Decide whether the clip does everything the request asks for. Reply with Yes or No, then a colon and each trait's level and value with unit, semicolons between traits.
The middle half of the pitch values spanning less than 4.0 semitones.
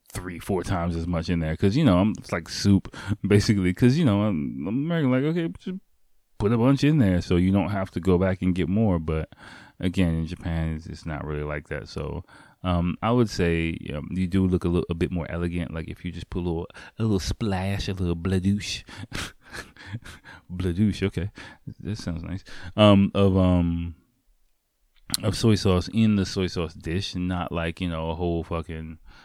Yes: average, 3.1 semitones